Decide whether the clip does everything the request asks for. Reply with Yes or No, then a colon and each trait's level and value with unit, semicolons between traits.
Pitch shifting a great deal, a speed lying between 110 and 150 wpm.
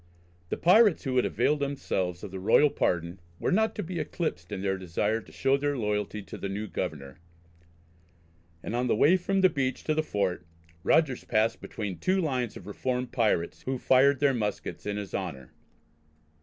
No: wide, 6.7 semitones; average, 185 wpm